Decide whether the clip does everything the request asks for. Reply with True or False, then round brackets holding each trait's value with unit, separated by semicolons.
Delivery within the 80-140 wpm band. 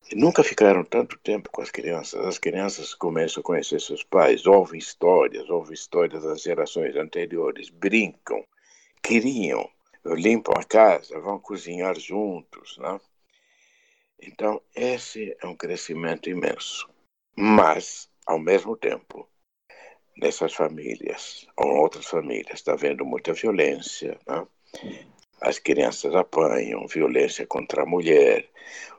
True (120 wpm)